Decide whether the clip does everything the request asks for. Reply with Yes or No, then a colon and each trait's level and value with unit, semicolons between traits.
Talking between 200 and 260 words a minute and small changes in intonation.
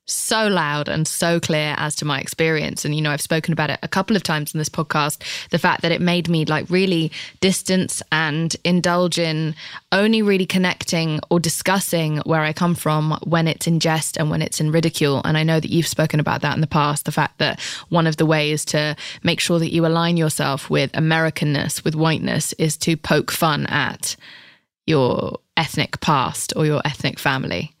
Yes: fast, 205 wpm; narrow, 1.9 semitones